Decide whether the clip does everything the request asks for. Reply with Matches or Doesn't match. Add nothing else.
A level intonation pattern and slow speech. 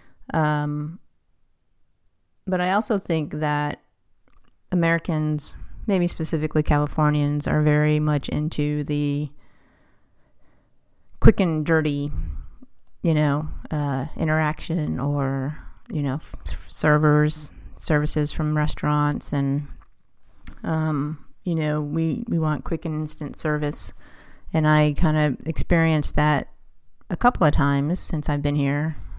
Matches